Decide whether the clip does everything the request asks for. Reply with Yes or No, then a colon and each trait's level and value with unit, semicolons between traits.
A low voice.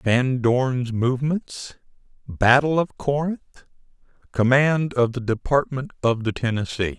Yes: low, 130 Hz